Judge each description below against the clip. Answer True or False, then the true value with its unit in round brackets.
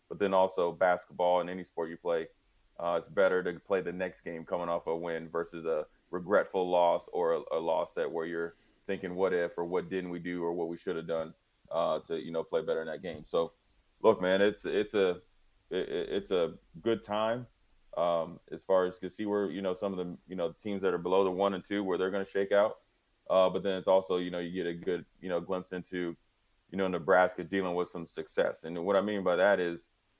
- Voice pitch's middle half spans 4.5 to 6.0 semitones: False (2.7 semitones)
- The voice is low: True (95 Hz)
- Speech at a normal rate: False (245 wpm)